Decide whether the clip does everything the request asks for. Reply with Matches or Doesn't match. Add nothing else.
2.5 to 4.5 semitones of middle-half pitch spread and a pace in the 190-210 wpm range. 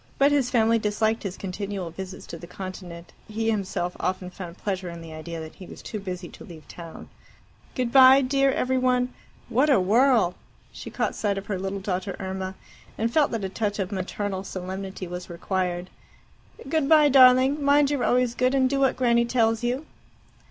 Doesn't match